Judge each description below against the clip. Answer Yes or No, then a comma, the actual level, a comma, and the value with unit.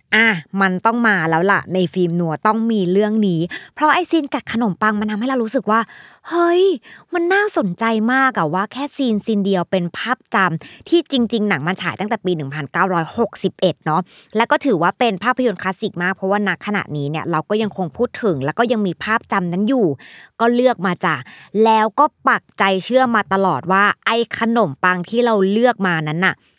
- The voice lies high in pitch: Yes, high, 210 Hz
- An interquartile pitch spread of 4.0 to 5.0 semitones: Yes, average, 4.3 semitones